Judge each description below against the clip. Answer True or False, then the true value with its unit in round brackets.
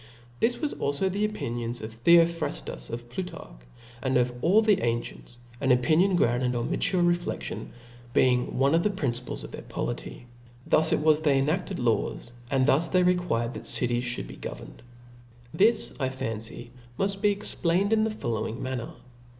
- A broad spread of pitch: True (7.1 semitones)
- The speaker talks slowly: False (180 wpm)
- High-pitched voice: False (140 Hz)